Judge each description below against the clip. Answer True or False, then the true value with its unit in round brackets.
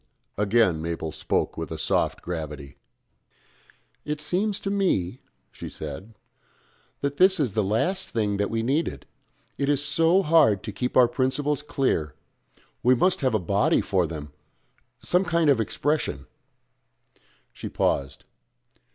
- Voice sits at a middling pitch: False (125 Hz)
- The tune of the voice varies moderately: False (8.0 semitones)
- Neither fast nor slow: True (145 wpm)